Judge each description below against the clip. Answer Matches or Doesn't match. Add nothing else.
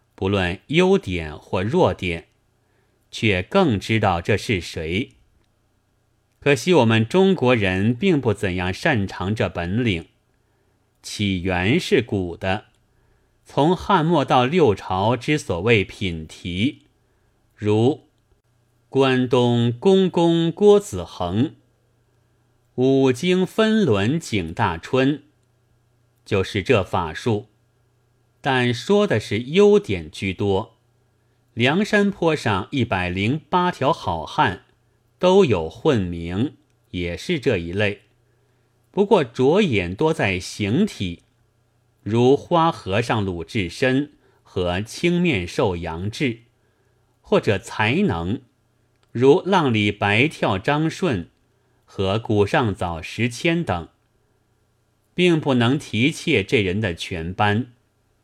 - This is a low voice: Matches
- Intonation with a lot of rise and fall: Doesn't match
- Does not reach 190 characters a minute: Matches